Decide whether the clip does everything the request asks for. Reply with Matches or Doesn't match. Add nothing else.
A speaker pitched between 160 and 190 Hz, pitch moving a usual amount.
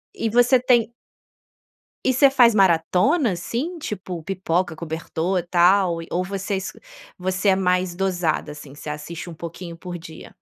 Matches